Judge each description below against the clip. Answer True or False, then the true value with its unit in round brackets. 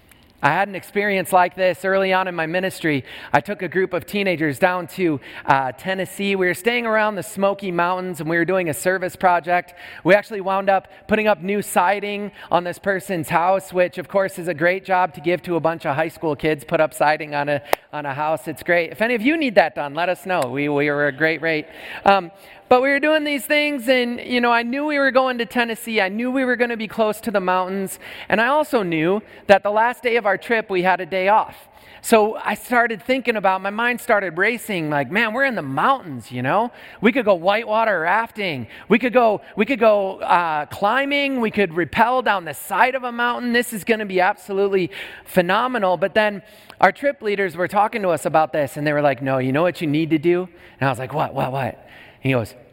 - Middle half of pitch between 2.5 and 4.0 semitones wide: False (4.5 semitones)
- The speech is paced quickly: True (240 wpm)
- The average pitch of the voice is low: False (190 Hz)